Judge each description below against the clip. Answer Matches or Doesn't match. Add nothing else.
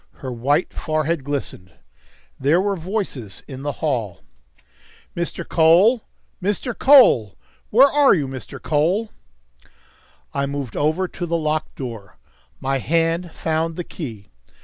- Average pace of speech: Doesn't match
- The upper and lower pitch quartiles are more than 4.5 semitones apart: Matches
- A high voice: Doesn't match